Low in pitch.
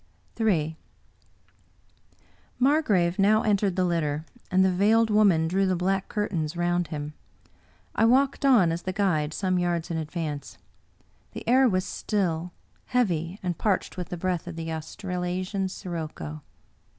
No: medium, 180 Hz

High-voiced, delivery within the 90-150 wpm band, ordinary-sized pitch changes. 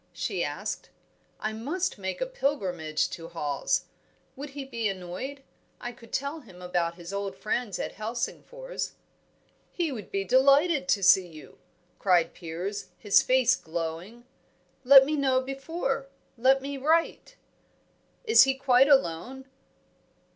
No: high, 245 Hz; average, 140 wpm; wide, 6.8 semitones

